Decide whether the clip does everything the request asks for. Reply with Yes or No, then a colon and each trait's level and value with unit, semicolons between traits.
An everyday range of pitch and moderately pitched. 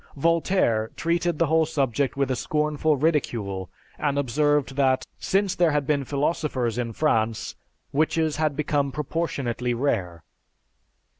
Yes: average, 4.0 semitones; medium, 145 Hz